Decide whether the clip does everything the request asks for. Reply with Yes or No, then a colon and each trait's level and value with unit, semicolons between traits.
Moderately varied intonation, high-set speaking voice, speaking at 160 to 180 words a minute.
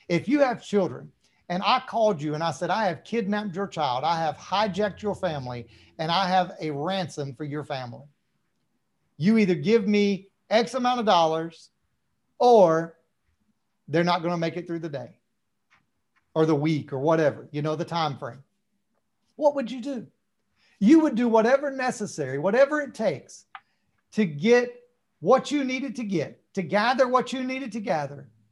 No: wide, 6.7 semitones; high, 195 Hz; average, 175 wpm